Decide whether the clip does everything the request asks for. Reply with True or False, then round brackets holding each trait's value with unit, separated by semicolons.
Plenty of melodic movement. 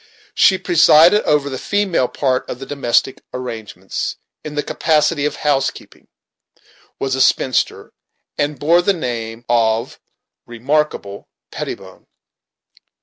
False (4.2 semitones)